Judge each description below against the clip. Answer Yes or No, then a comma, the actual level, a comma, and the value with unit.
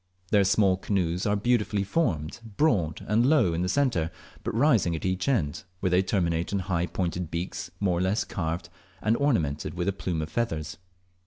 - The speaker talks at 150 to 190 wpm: Yes, average, 185 wpm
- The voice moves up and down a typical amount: Yes, average, 4.1 semitones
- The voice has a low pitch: Yes, very low, 95 Hz